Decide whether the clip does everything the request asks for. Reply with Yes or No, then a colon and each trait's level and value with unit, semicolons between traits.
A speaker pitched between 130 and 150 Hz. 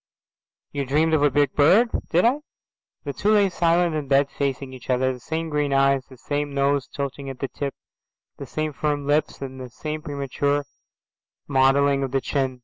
Yes: medium, 140 Hz